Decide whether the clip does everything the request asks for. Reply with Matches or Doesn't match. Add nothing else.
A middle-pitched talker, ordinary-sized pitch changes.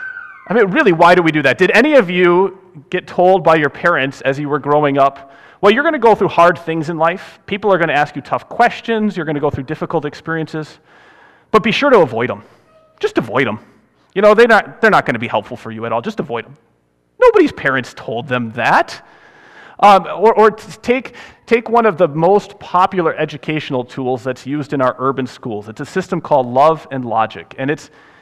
Doesn't match